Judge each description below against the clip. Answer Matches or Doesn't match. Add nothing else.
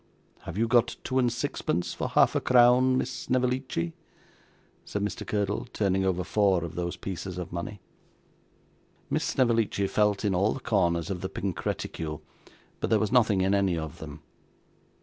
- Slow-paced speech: Doesn't match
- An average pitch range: Matches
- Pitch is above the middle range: Doesn't match